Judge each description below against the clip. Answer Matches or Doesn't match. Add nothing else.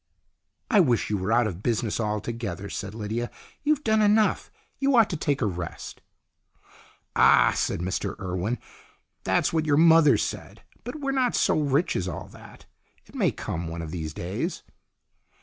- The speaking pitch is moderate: Doesn't match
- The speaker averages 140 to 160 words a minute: Doesn't match